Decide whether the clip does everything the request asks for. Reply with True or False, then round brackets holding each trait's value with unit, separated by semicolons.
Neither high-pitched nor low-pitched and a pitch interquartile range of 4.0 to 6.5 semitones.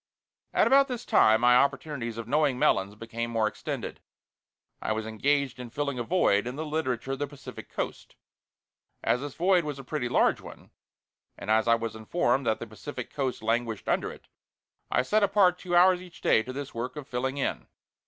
False (130 Hz; 4.6 semitones)